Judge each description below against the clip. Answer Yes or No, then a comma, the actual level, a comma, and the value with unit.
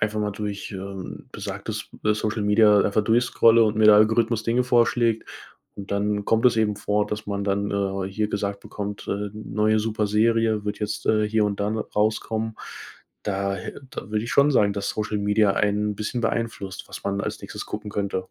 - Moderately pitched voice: No, low, 105 Hz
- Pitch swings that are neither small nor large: No, narrow, 1.5 semitones